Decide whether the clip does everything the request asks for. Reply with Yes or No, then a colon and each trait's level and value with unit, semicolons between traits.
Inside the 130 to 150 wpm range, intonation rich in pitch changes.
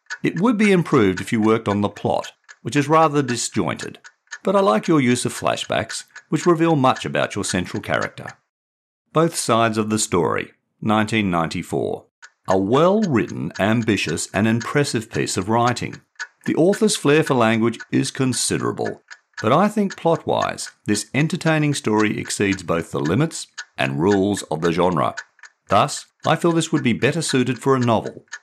No: average, 165 wpm; wide, 7.3 semitones